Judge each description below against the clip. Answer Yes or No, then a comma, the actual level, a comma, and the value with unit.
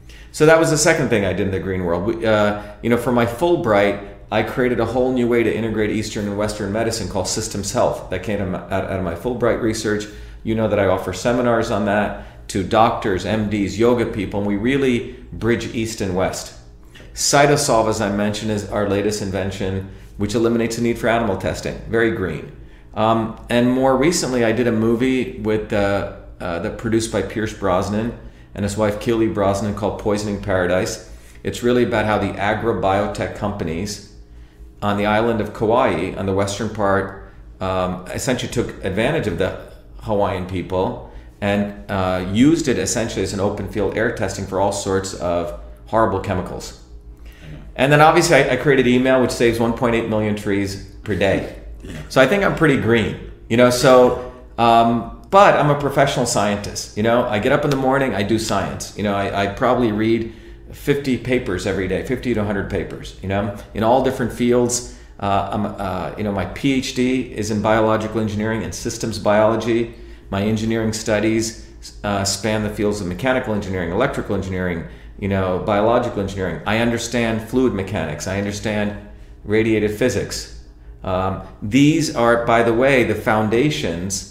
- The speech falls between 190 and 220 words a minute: No, average, 175 wpm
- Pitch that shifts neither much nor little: Yes, average, 3.2 semitones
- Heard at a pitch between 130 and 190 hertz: No, low, 105 Hz